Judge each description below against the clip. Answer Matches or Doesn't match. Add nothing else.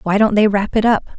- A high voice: Matches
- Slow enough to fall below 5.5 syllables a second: Doesn't match